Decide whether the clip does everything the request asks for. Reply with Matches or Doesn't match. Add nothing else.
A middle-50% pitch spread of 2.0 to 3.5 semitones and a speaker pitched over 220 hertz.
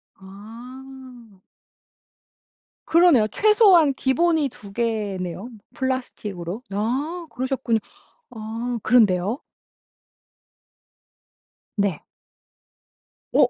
Doesn't match